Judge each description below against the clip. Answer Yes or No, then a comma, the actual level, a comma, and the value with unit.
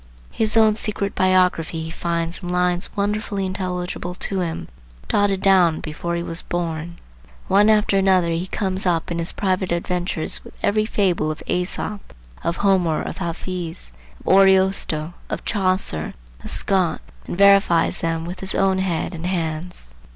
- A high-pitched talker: No, medium, 180 Hz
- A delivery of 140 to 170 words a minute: Yes, average, 155 wpm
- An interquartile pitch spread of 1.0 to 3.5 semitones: Yes, narrow, 2.4 semitones